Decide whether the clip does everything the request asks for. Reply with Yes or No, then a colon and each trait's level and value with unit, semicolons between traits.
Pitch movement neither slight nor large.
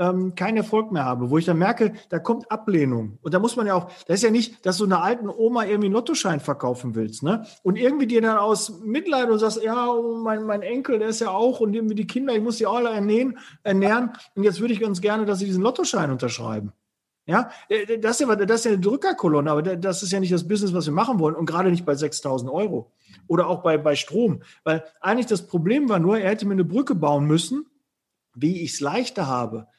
No: wide, 5.9 semitones